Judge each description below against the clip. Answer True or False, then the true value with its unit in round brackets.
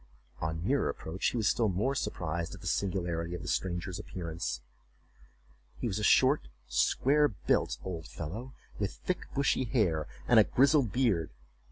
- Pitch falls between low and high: False (95 Hz)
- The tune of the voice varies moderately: False (6.6 semitones)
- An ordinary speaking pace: True (160 wpm)